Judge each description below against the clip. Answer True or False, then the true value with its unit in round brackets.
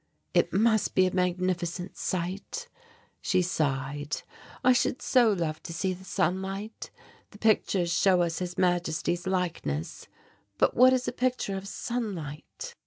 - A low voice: False (185 Hz)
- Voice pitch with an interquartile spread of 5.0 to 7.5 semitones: False (3.2 semitones)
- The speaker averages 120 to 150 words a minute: True (140 wpm)